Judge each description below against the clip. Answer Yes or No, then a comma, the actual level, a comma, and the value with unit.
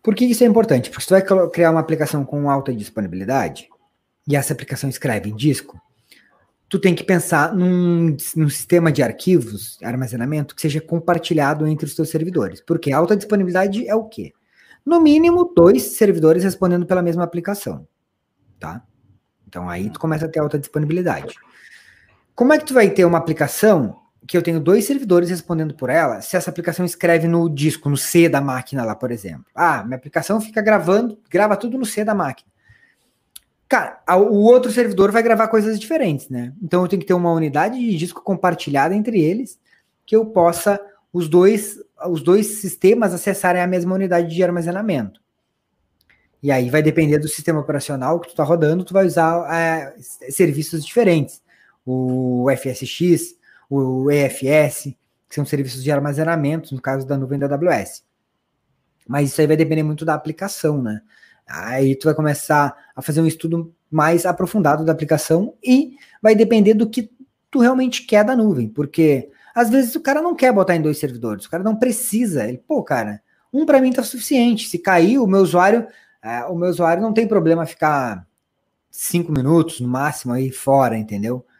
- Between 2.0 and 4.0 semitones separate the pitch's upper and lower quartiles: No, wide, 5.4 semitones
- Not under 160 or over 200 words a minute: Yes, average, 180 wpm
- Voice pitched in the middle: Yes, medium, 170 Hz